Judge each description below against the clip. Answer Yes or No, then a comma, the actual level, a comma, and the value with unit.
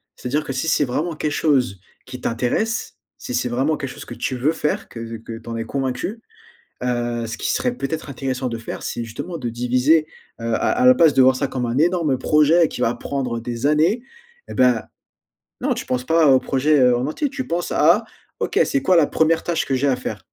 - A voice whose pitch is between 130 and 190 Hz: Yes, low, 135 Hz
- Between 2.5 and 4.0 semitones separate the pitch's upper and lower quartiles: No, average, 4.6 semitones